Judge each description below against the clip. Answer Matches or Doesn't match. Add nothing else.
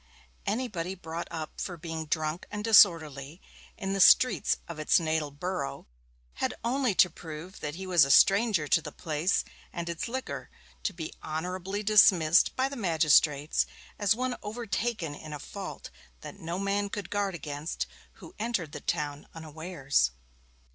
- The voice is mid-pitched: Matches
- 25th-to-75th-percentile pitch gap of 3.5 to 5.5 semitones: Matches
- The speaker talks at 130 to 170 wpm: Matches